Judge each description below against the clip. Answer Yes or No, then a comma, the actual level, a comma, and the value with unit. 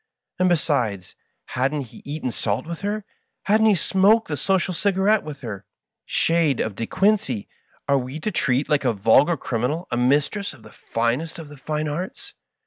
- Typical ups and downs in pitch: No, wide, 6.6 semitones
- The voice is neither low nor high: Yes, medium, 150 Hz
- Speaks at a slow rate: No, average, 180 wpm